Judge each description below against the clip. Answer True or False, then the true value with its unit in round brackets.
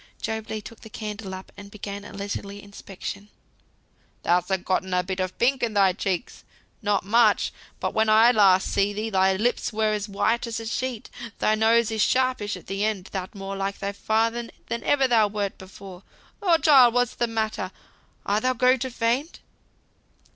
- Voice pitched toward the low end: False (210 Hz)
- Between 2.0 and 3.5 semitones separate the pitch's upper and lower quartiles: True (2.8 semitones)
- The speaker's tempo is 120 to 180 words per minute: False (190 wpm)